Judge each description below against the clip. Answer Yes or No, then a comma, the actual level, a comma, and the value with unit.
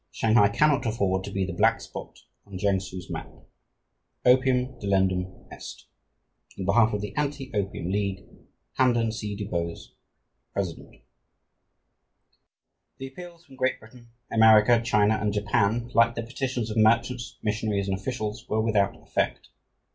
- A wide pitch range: No, average, 3.3 semitones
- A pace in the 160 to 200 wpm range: No, slow, 135 wpm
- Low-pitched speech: Yes, low, 110 Hz